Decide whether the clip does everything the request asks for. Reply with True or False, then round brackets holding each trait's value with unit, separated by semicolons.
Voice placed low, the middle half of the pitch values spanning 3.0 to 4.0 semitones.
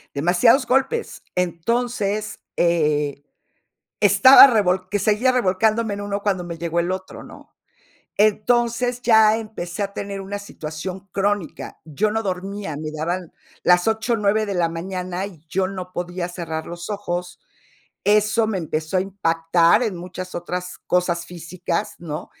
False (185 Hz; 3.6 semitones)